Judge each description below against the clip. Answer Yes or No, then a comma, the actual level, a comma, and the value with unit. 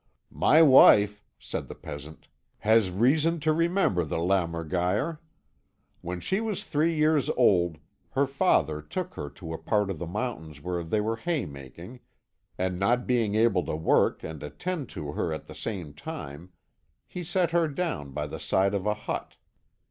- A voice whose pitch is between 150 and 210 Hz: No, low, 100 Hz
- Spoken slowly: No, average, 170 wpm